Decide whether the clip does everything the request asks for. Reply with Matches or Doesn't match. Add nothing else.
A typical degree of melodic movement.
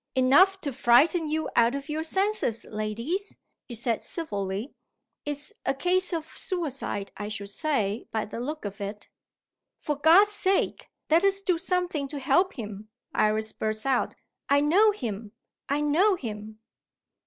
Doesn't match